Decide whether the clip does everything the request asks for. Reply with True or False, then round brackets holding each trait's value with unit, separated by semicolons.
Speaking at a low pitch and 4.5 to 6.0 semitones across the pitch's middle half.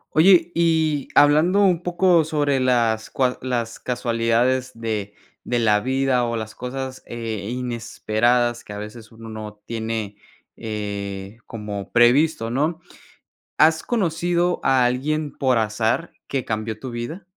True (120 Hz; 5.1 semitones)